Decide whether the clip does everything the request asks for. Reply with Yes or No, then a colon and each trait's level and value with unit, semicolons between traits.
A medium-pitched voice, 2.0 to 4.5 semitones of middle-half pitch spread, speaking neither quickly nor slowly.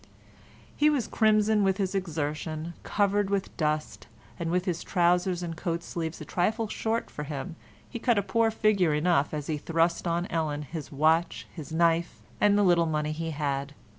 Yes: medium, 170 Hz; average, 4.2 semitones; average, 180 wpm